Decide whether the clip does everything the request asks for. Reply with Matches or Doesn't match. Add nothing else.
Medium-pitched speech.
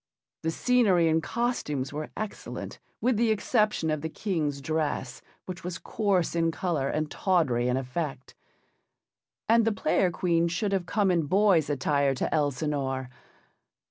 Matches